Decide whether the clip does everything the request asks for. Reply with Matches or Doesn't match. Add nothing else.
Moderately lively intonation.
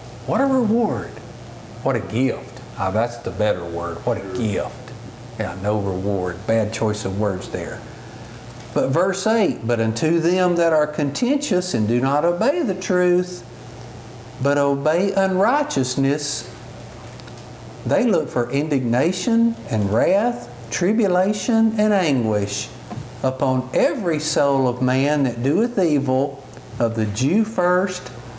Doesn't match